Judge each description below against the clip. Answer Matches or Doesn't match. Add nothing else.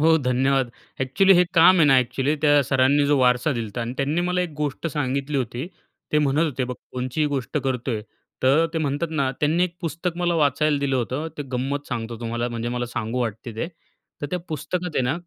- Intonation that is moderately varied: Matches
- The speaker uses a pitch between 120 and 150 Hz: Matches